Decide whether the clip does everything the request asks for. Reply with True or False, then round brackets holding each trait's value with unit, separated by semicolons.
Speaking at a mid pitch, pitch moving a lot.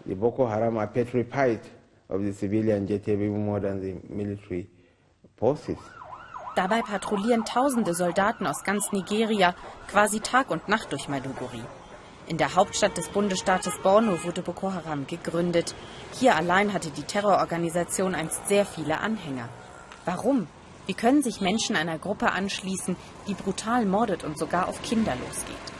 True (175 Hz; 8.9 semitones)